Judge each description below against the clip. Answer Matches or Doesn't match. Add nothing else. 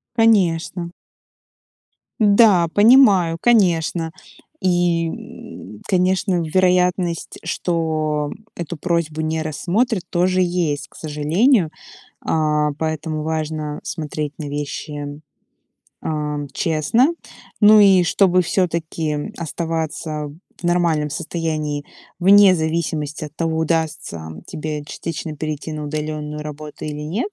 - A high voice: Doesn't match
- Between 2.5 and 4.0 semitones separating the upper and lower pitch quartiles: Matches